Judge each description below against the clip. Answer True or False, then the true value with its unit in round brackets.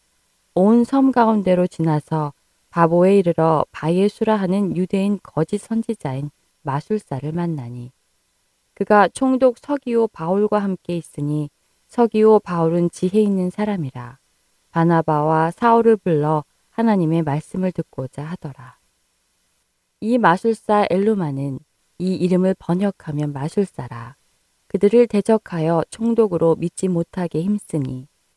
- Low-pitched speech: False (175 Hz)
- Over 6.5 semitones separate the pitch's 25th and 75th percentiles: False (5.3 semitones)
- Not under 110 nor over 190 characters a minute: False (270 characters per minute)